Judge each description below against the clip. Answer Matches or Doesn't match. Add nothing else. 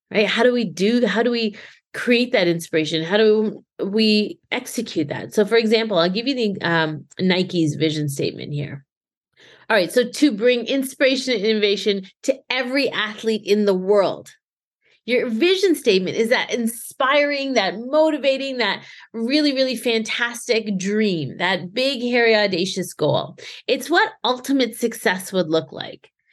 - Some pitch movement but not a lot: Matches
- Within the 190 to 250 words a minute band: Doesn't match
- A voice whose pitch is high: Matches